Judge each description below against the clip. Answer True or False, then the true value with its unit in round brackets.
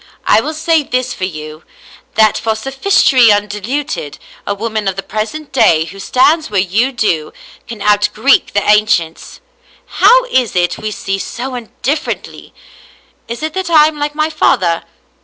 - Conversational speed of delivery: True (170 wpm)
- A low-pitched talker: False (220 Hz)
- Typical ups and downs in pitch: False (6.7 semitones)